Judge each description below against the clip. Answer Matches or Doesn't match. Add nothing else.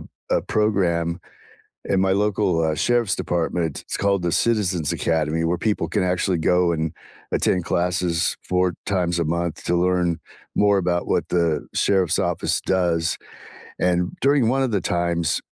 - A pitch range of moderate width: Doesn't match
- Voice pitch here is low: Matches